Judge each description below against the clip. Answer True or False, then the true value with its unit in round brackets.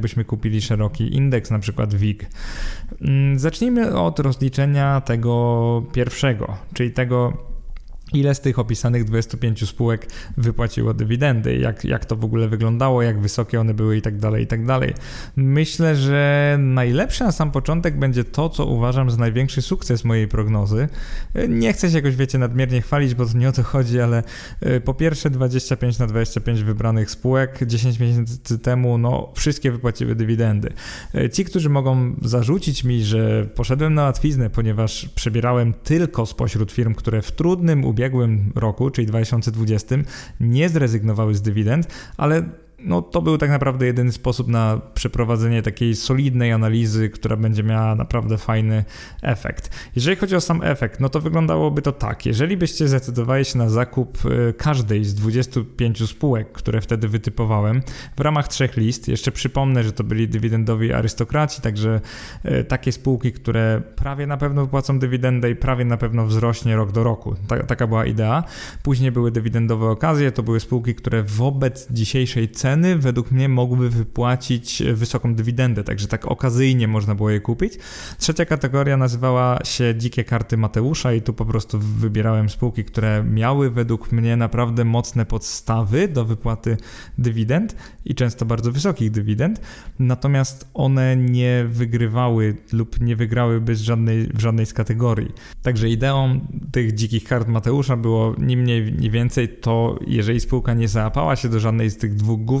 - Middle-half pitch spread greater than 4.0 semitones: False (2.9 semitones)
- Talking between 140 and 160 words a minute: True (155 wpm)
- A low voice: True (120 Hz)